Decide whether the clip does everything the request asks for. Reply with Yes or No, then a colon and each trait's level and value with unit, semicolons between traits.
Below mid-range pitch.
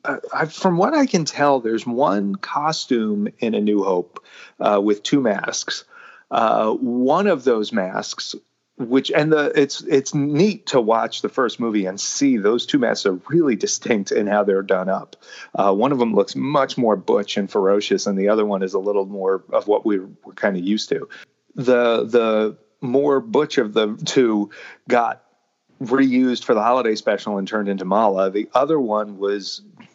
Yes: low, 115 Hz